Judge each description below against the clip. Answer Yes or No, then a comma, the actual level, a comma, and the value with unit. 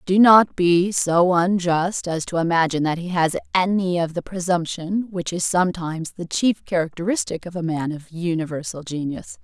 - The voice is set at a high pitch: No, medium, 175 Hz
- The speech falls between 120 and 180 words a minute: Yes, average, 170 wpm